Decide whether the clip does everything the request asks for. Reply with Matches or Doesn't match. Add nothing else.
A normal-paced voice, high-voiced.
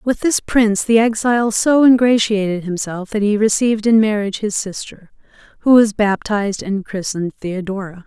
Matches